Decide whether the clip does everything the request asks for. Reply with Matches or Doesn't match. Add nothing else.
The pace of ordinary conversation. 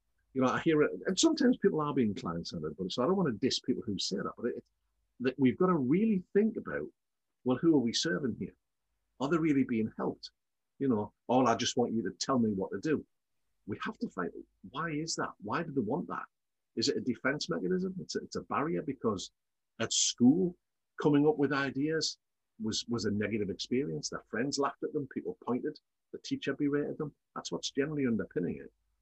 Doesn't match